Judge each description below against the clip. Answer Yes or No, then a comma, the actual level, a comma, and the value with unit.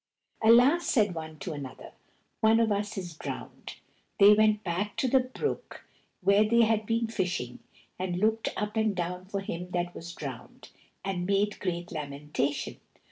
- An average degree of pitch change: Yes, average, 4.2 semitones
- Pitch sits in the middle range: No, high, 200 Hz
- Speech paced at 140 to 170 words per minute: Yes, average, 160 wpm